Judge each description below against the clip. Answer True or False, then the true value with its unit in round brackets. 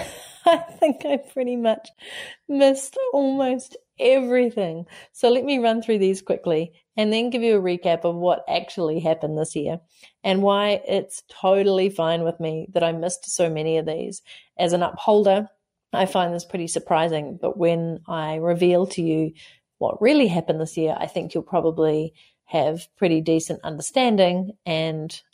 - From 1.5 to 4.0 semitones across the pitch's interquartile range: False (5.6 semitones)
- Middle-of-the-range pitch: True (180 Hz)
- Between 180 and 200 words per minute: False (165 wpm)